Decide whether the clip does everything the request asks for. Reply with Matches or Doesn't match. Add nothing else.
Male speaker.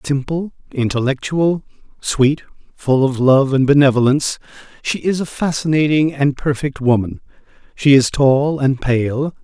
Matches